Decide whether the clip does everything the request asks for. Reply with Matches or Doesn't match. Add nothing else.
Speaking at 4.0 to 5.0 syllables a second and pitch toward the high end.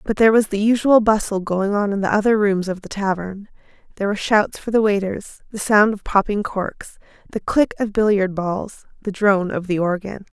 Doesn't match